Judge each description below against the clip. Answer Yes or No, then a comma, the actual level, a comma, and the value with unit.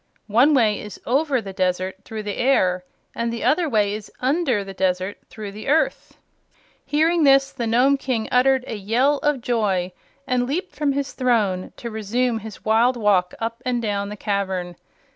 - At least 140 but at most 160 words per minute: No, average, 180 wpm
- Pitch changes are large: No, average, 4.8 semitones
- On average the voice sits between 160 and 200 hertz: No, high, 230 Hz